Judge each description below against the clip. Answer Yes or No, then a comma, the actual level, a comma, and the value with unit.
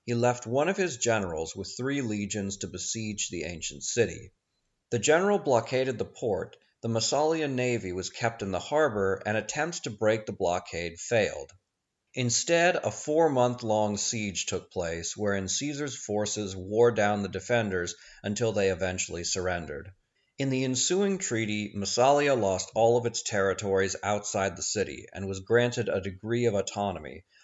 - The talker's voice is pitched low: Yes, low, 105 Hz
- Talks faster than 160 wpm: No, average, 155 wpm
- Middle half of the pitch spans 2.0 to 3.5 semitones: No, average, 4.2 semitones